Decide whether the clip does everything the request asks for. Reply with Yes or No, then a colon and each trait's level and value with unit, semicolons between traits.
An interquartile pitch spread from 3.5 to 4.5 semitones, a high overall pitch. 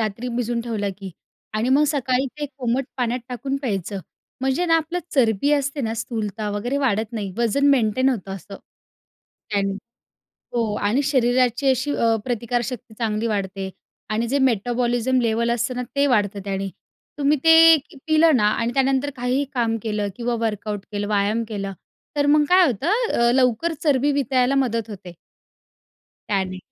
Yes: average, 4.1 semitones; high, 240 Hz